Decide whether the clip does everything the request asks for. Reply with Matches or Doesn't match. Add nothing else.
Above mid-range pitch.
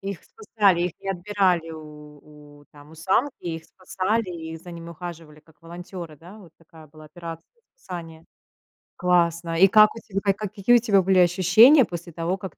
Doesn't match